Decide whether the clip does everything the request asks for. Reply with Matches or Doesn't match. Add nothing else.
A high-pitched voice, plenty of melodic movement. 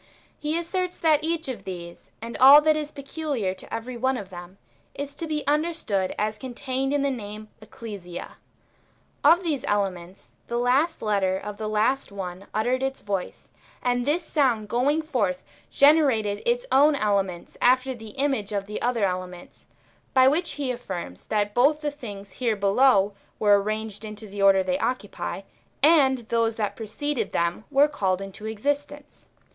Matches